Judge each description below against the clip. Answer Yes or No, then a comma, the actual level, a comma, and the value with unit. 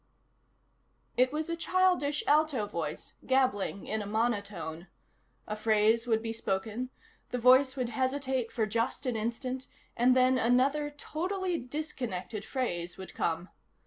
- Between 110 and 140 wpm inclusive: Yes, slow, 135 wpm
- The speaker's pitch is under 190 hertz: No, high, 245 Hz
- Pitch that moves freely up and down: No, average, 4.2 semitones